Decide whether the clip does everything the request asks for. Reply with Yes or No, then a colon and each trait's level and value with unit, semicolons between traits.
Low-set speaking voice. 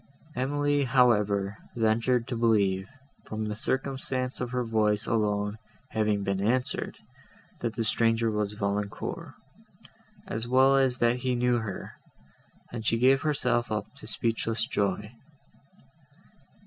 Yes: low, 115 Hz